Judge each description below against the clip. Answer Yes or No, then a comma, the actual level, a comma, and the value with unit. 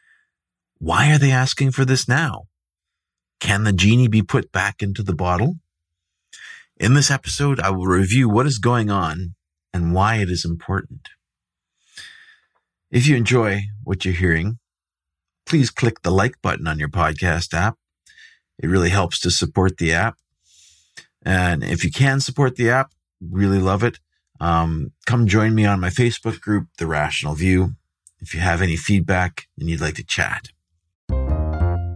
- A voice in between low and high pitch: No, very low, 95 Hz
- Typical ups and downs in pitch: No, wide, 6.1 semitones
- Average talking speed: Yes, average, 160 wpm